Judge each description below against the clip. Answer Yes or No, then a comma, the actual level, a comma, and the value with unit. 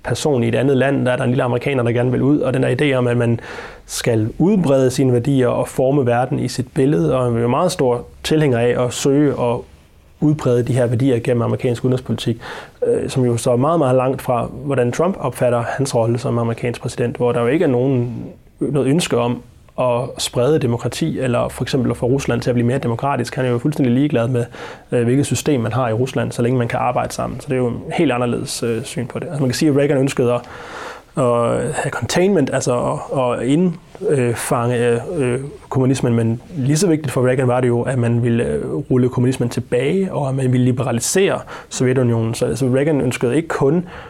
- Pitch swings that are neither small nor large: No, narrow, 2.2 semitones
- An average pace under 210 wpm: No, average, 215 wpm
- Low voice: Yes, low, 125 Hz